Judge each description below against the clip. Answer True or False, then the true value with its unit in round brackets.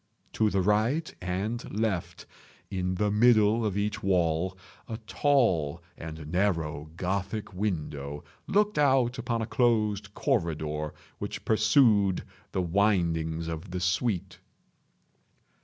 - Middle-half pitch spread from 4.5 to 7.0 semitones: True (4.8 semitones)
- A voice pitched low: True (100 Hz)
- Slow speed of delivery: True (115 wpm)